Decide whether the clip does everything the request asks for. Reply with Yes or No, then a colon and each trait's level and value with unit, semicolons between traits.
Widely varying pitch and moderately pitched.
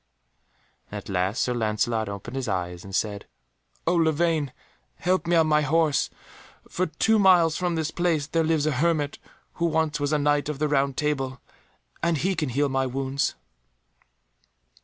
No: average, 3.8 semitones; medium, 150 Hz